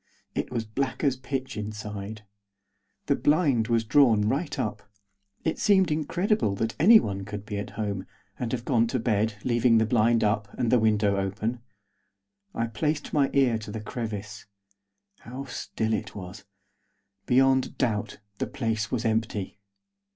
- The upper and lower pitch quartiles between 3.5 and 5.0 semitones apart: Yes, average, 3.8 semitones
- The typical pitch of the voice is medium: No, low, 115 Hz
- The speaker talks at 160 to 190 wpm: No, average, 150 wpm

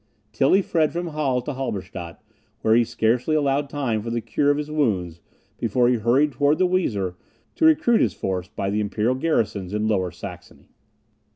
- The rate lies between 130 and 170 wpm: No, average, 180 wpm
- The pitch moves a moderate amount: No, wide, 6.0 semitones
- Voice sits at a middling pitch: No, low, 120 Hz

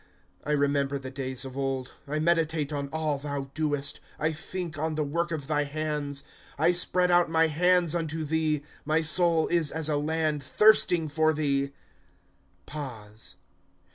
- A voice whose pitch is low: No, medium, 155 Hz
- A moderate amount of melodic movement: No, narrow, 2.2 semitones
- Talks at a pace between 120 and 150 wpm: No, average, 170 wpm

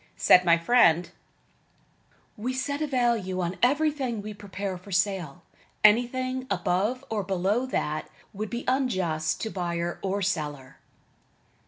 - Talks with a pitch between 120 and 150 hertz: No, high, 200 Hz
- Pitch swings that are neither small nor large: No, wide, 5.7 semitones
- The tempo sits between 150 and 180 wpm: No, slow, 135 wpm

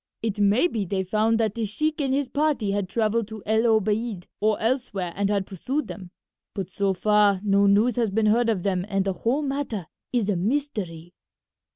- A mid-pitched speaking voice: No, high, 215 Hz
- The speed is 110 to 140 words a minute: No, average, 200 wpm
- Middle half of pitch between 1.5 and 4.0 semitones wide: Yes, average, 3.0 semitones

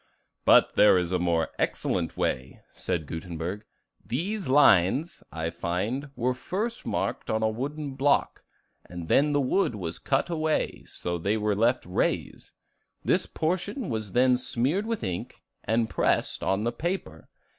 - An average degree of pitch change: No, wide, 8.6 semitones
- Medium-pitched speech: No, low, 115 Hz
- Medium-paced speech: Yes, average, 155 wpm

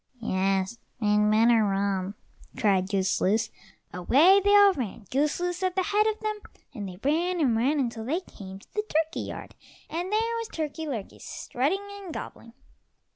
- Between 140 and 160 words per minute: No, average, 175 wpm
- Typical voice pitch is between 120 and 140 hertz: No, very high, 265 Hz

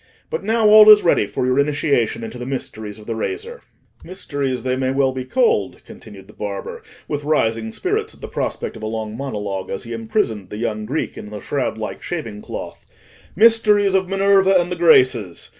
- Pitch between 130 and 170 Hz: Yes, low, 135 Hz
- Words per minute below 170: No, average, 195 wpm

